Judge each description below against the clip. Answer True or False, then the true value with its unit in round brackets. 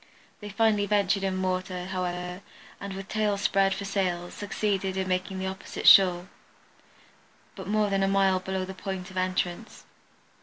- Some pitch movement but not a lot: False (1.4 semitones)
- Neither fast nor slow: True (165 wpm)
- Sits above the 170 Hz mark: True (190 Hz)